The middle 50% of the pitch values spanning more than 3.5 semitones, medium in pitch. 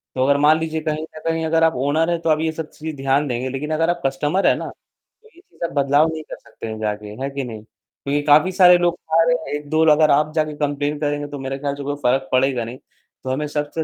No: average, 2.8 semitones; medium, 150 Hz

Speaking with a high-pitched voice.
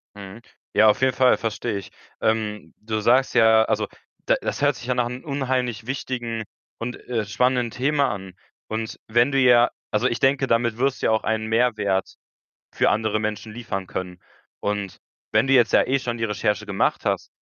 No: low, 115 Hz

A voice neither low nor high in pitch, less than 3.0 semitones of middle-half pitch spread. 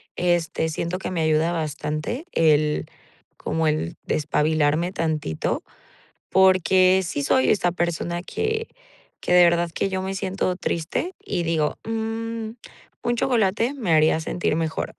No: medium, 175 Hz; average, 3.5 semitones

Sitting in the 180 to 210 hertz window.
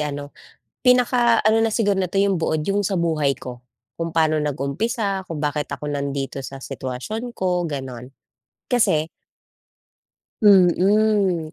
No: medium, 170 Hz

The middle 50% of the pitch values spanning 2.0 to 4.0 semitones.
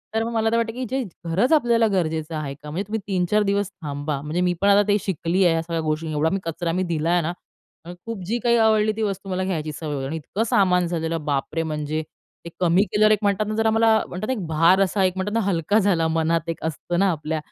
No: average, 4.4 semitones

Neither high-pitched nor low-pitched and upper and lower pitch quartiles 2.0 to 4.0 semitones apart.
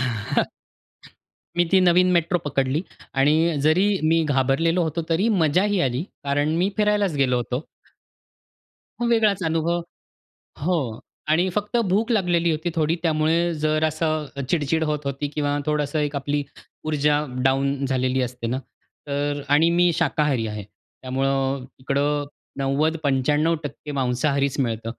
Yes: medium, 150 Hz; average, 3.5 semitones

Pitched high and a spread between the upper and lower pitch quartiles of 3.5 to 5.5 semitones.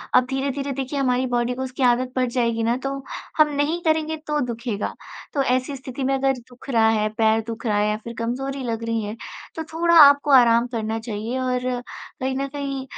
No: very high, 255 Hz; average, 3.0 semitones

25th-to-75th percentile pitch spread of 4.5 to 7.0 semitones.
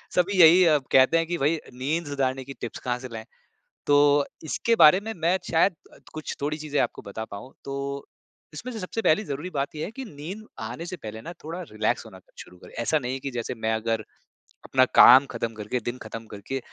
Yes: wide, 5.5 semitones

